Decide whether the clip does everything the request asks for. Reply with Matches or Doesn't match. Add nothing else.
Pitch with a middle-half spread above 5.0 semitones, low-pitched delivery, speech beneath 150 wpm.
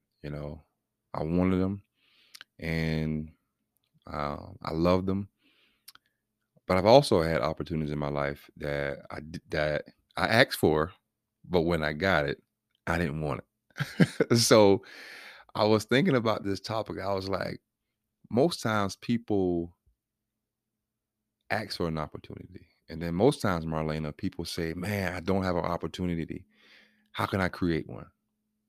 Matches